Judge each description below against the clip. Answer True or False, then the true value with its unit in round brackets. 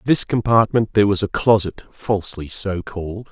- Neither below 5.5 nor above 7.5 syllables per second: False (5.3 syllables/s)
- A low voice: True (105 Hz)